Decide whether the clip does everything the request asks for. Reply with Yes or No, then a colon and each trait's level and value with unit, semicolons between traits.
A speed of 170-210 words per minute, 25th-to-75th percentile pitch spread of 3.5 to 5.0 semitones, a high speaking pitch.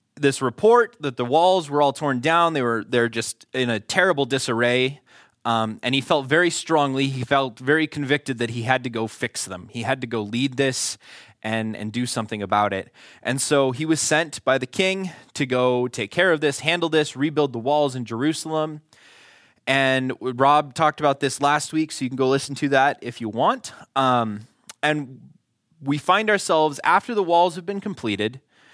No: average, 200 wpm; average, 4.0 semitones; low, 135 Hz